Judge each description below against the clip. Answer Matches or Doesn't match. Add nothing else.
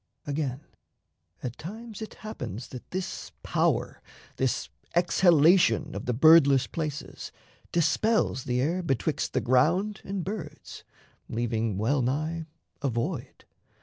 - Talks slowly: Matches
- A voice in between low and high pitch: Matches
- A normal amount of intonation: Doesn't match